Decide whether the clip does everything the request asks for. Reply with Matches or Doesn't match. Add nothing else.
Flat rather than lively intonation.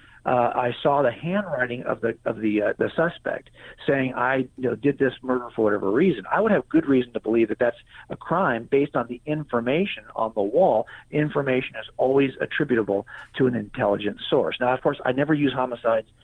Doesn't match